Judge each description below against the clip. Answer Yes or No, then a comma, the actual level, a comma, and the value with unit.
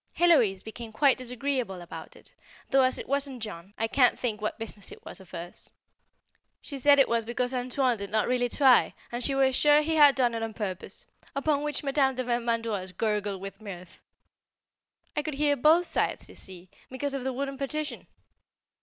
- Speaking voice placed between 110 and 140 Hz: No, very high, 250 Hz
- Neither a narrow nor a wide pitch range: Yes, average, 4.4 semitones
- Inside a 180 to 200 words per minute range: Yes, average, 190 wpm